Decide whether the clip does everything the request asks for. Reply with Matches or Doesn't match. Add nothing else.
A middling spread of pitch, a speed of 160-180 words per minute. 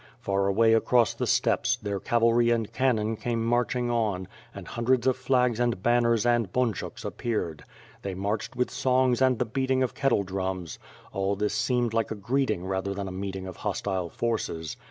Matches